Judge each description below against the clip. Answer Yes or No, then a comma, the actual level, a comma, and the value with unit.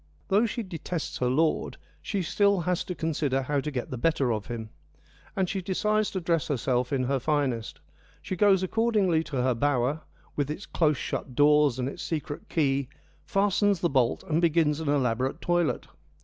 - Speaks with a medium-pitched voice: Yes, medium, 150 Hz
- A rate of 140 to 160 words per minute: No, average, 185 wpm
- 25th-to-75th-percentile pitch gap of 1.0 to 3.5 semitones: No, average, 5.2 semitones